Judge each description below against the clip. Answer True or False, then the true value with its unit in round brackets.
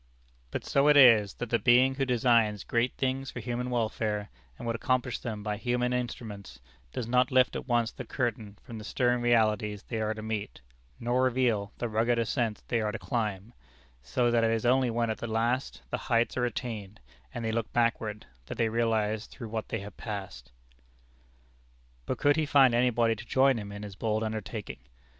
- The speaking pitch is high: False (115 Hz)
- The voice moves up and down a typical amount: False (2.3 semitones)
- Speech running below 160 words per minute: False (195 wpm)